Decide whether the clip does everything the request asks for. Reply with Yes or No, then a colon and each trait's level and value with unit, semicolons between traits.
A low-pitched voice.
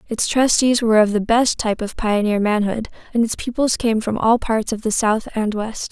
No: high, 220 Hz